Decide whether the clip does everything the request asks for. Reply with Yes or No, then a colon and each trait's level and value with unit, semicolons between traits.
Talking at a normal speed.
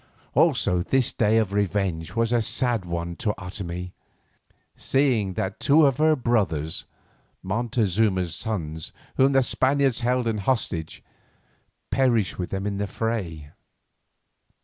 No: slow, 125 wpm